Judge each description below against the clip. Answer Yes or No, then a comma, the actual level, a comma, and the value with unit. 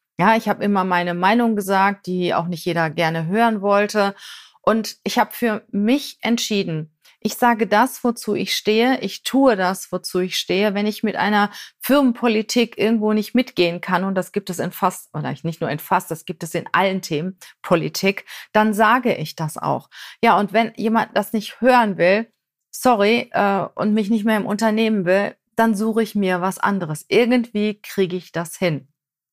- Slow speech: No, fast, 190 wpm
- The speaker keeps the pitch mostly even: No, average, 3.6 semitones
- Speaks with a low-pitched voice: No, high, 205 Hz